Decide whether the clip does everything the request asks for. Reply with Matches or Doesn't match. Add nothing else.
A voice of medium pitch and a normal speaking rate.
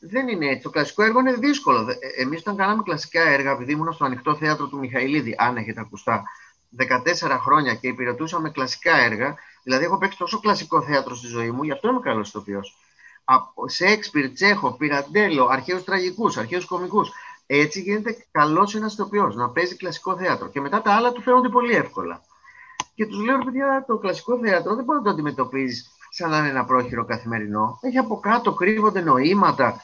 Doesn't match